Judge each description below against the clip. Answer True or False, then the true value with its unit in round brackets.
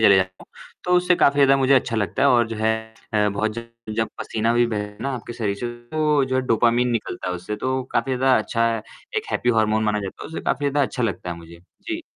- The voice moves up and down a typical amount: True (3.9 semitones)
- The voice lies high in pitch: False (115 Hz)